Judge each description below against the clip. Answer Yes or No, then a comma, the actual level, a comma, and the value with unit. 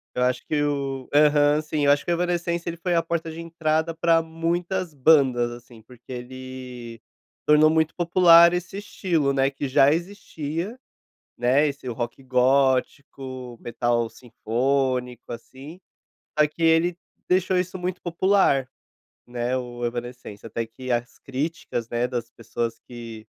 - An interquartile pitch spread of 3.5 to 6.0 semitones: Yes, average, 5.1 semitones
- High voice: No, medium, 140 Hz